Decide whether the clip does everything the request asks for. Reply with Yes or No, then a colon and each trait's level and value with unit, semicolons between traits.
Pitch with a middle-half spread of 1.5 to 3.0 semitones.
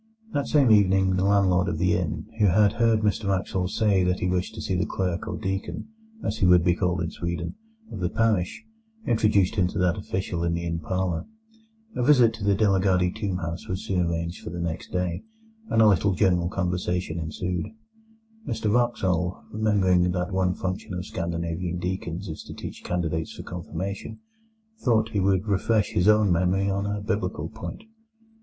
Yes: narrow, 2.6 semitones